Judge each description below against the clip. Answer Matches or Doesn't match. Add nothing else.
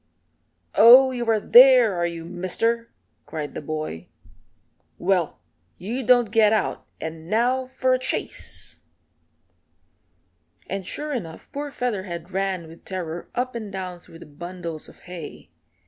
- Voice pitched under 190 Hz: Doesn't match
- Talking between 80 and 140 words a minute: Matches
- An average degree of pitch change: Doesn't match